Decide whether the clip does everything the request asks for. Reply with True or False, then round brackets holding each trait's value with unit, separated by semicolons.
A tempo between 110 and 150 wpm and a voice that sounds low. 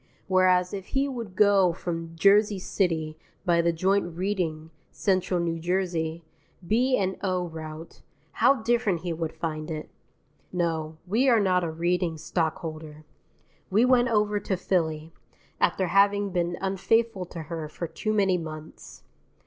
False (140 wpm; 180 Hz)